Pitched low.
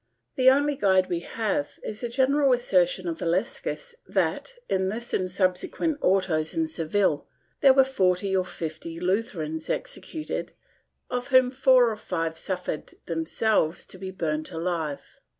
No: high, 190 Hz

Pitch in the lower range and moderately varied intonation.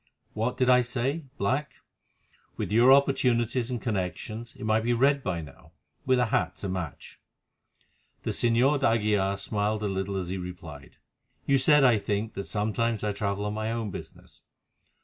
Yes: low, 110 Hz; average, 4.1 semitones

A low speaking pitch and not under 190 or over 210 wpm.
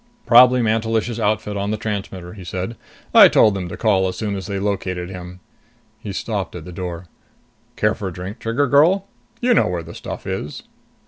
Yes: low, 100 Hz; average, 195 wpm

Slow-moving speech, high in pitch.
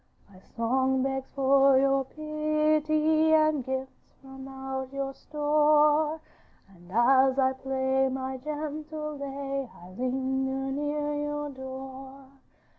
Yes: slow, 115 wpm; very high, 270 Hz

